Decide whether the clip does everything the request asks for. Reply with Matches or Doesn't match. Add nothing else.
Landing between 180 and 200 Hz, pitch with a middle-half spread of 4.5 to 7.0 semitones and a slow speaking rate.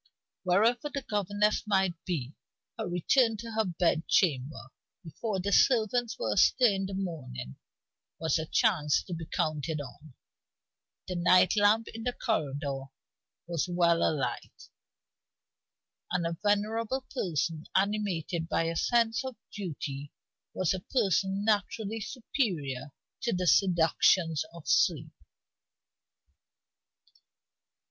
Matches